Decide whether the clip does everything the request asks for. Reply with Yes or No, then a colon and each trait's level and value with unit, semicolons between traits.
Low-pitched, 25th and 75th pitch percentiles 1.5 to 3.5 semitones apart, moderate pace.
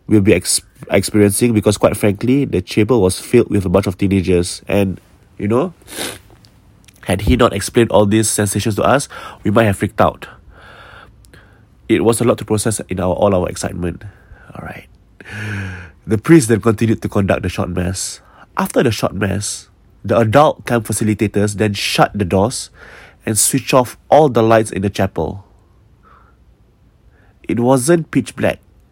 Yes: low, 105 Hz; average, 2.9 semitones; average, 165 wpm